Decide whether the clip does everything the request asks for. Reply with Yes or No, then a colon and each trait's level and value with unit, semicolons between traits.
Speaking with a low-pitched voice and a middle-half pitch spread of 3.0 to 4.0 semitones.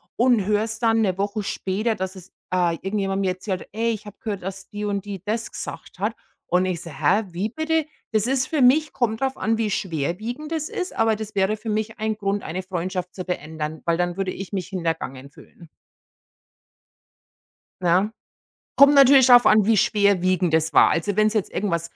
No: high, 200 Hz; average, 3.5 semitones